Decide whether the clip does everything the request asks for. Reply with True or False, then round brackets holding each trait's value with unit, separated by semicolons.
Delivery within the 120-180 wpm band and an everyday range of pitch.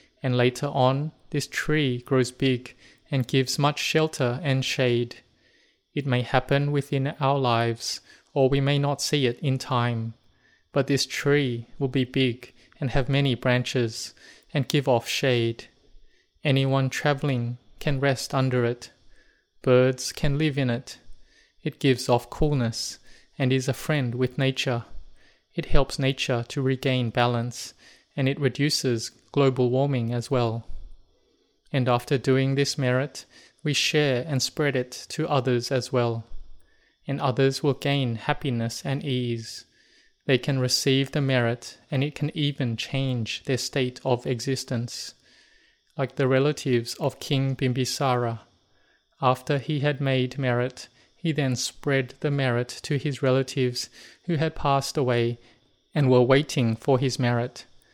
False (145 wpm; 2.3 semitones)